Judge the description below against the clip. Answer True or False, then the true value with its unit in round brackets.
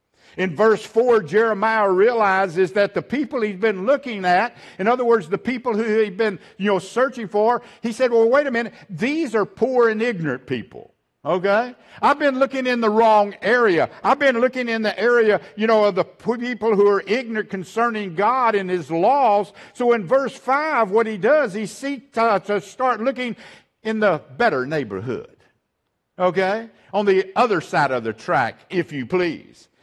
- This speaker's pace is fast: False (185 wpm)